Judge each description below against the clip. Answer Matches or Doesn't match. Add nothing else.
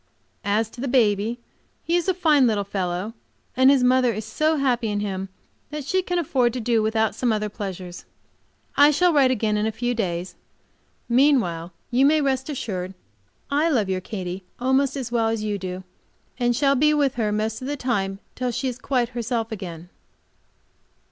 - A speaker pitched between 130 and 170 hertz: Doesn't match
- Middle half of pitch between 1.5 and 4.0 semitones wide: Doesn't match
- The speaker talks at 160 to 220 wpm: Matches